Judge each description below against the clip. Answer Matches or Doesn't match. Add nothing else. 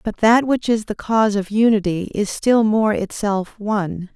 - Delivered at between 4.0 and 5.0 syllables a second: Matches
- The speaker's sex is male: Doesn't match